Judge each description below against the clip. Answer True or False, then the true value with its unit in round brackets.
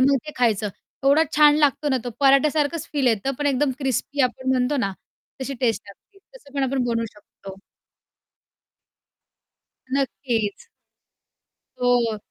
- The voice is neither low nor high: False (265 Hz)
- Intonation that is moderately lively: True (3.6 semitones)